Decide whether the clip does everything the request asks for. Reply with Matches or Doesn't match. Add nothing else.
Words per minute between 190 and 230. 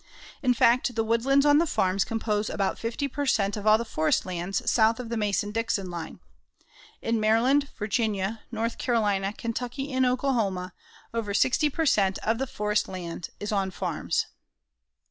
Doesn't match